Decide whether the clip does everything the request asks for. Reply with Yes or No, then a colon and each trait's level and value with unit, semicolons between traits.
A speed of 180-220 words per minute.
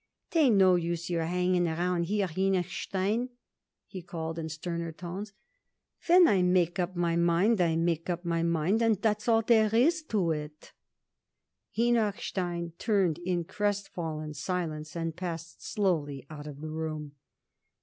No: average, 145 wpm